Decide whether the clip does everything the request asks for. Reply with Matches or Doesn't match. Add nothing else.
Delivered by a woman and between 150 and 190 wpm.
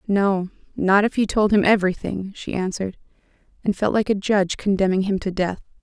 Matches